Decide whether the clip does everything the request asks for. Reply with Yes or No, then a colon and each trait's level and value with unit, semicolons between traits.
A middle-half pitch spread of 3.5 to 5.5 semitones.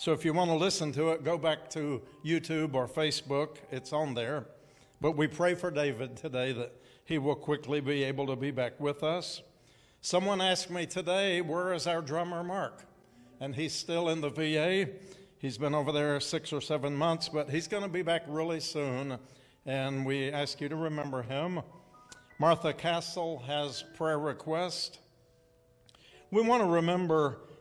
No: average, 3.0 semitones